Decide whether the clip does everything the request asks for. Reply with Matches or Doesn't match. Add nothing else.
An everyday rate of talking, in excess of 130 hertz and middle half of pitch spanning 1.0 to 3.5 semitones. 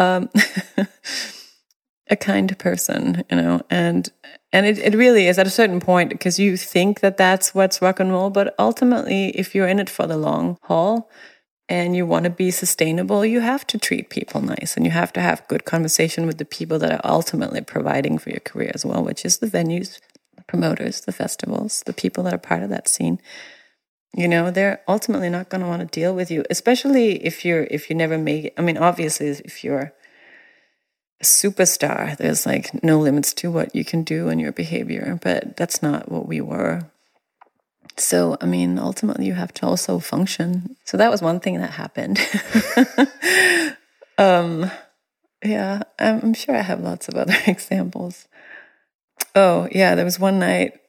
Doesn't match